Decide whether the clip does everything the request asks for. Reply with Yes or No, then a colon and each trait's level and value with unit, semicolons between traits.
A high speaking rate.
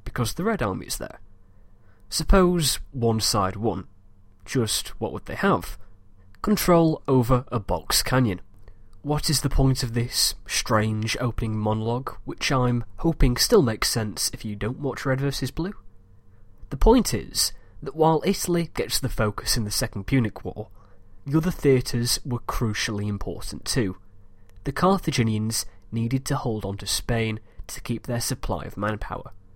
No: average, 155 wpm